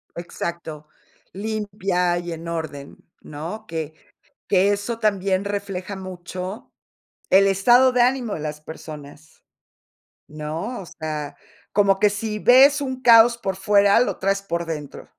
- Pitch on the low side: No, high, 195 Hz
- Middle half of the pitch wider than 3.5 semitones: Yes, average, 4.4 semitones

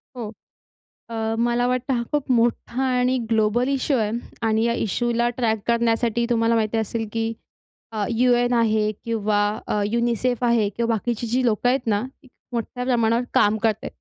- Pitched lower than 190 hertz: No, high, 235 Hz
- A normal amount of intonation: No, narrow, 1.7 semitones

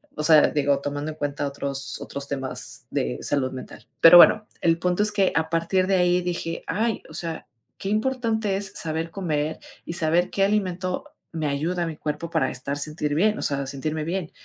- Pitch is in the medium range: Yes, medium, 165 Hz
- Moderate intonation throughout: Yes, average, 4.2 semitones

